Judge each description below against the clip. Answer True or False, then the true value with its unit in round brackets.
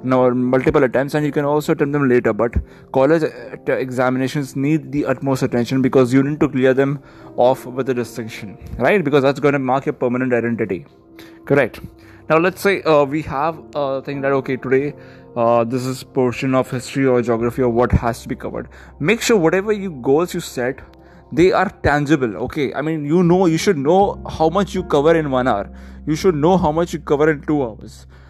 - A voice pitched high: False (135 Hz)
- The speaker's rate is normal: False (210 wpm)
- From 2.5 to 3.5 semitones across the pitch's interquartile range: False (3.9 semitones)